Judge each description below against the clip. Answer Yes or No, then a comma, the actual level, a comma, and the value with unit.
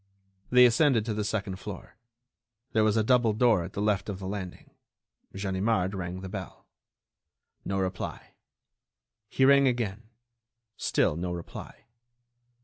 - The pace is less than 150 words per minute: Yes, average, 140 wpm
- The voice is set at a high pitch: No, low, 105 Hz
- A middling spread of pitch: Yes, average, 3.3 semitones